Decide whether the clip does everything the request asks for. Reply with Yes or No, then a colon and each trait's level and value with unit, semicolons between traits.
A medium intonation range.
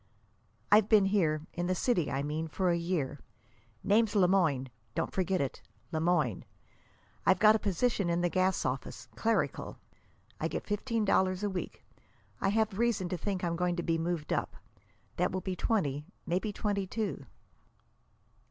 Yes: average, 3.5 semitones